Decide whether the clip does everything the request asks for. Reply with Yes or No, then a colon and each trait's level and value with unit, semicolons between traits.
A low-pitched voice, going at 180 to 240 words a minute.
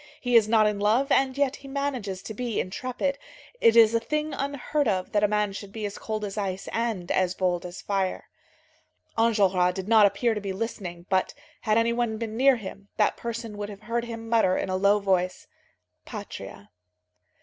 No: high, 215 Hz; average, 200 wpm